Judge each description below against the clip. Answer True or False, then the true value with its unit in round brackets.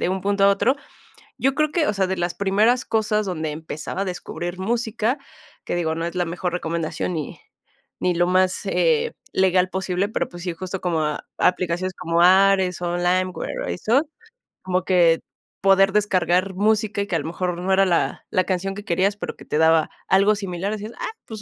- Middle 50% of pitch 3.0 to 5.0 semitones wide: False (2.5 semitones)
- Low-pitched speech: False (185 Hz)